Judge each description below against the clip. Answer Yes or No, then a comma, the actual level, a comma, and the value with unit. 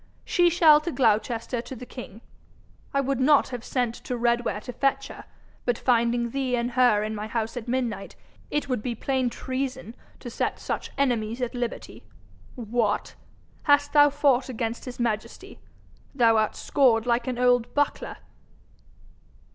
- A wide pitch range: No, narrow, 2.5 semitones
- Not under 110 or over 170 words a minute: Yes, average, 160 wpm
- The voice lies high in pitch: Yes, high, 245 Hz